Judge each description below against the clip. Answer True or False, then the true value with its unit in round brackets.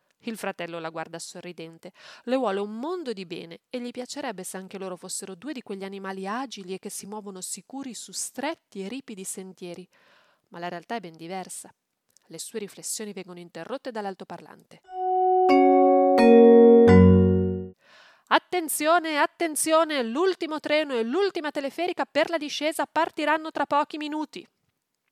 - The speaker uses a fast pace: False (140 wpm)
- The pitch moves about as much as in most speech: False (8.4 semitones)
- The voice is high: True (225 Hz)